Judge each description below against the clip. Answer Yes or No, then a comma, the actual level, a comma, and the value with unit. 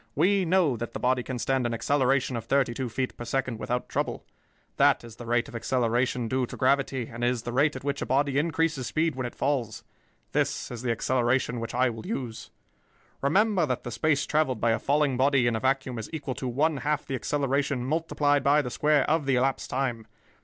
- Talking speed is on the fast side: Yes, fast, 215 wpm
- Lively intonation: No, average, 3.0 semitones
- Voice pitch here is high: No, low, 130 Hz